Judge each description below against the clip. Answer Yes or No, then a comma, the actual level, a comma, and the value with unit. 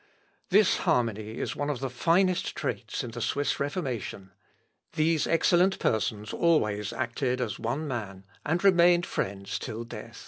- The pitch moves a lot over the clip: Yes, wide, 7.2 semitones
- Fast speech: No, average, 145 wpm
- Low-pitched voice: Yes, low, 130 Hz